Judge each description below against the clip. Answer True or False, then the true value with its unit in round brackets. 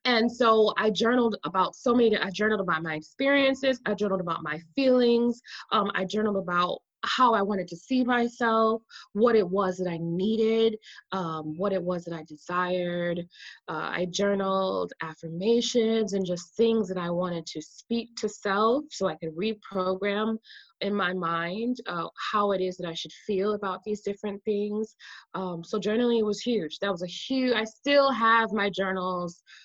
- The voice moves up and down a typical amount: True (3.9 semitones)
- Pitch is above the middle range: True (205 Hz)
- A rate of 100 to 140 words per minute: False (175 wpm)